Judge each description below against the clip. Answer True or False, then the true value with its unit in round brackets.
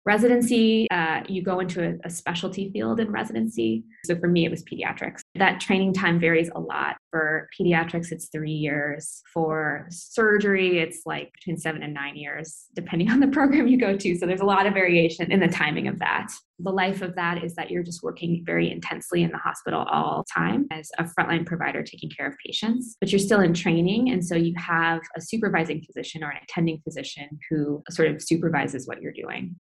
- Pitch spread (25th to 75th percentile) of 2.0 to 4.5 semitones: True (2.9 semitones)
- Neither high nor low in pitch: True (170 Hz)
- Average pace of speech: False (210 wpm)